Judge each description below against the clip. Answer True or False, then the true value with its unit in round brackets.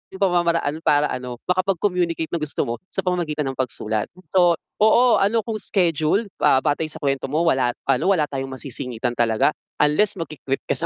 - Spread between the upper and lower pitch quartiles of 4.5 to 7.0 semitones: True (5.3 semitones)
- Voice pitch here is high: False (155 Hz)